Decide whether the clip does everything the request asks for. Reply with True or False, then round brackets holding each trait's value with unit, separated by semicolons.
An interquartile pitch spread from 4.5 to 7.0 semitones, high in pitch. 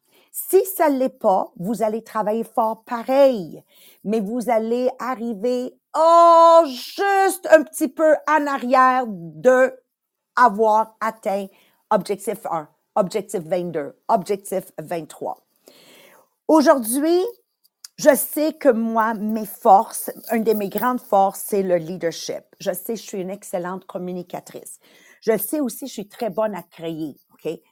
True (5.3 semitones; 225 Hz)